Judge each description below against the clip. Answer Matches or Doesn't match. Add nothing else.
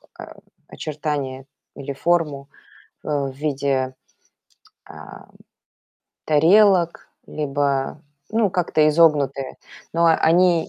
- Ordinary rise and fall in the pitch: Matches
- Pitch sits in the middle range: Matches